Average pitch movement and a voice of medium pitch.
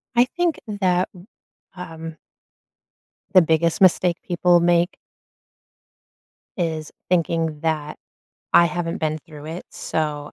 No: narrow, 2.2 semitones; medium, 170 Hz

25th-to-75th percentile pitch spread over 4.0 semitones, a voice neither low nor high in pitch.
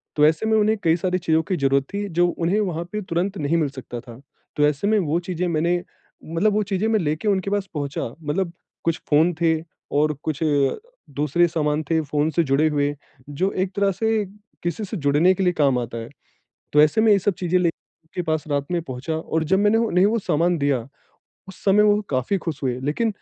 Yes: average, 4.5 semitones; medium, 170 Hz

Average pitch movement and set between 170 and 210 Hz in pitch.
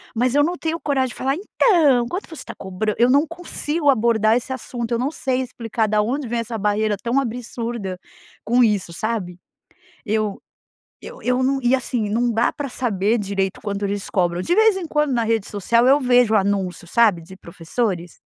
No: average, 4.3 semitones; high, 235 Hz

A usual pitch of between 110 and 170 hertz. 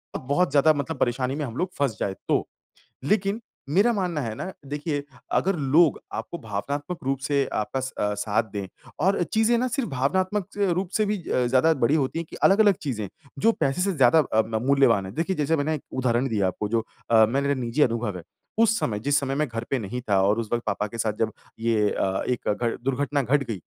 Yes: low, 135 Hz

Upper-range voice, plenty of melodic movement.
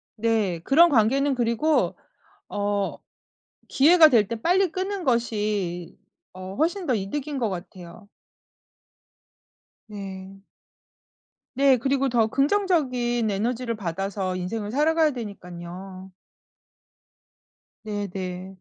Yes: high, 225 Hz; wide, 6.1 semitones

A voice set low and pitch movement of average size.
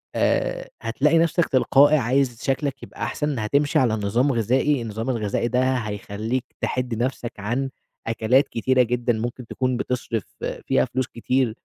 Yes: low, 125 Hz; average, 3.0 semitones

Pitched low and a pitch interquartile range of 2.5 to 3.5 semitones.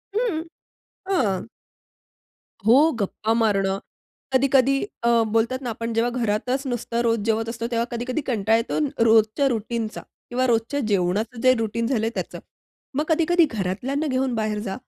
No: high, 230 Hz; average, 3.0 semitones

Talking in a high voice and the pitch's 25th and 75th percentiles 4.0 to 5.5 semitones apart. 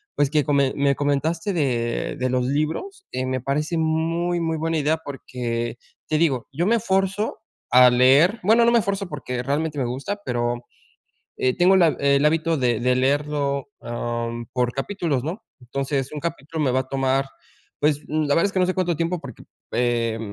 No: medium, 145 Hz; average, 4.7 semitones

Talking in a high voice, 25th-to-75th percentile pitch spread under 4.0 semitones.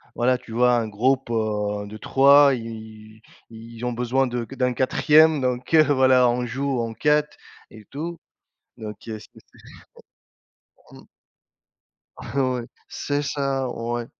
No: low, 125 Hz; average, 3.1 semitones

